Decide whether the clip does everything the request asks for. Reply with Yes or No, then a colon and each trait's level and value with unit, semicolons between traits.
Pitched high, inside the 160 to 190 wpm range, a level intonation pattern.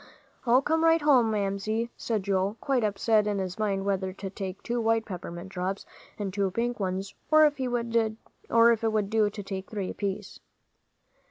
No: high, 210 Hz; average, 170 wpm; average, 3.2 semitones